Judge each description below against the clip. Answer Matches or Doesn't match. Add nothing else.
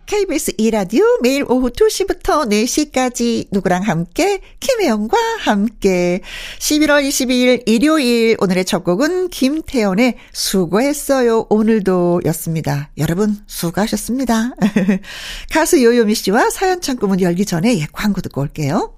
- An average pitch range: Doesn't match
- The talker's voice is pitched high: Matches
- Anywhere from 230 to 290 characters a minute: Matches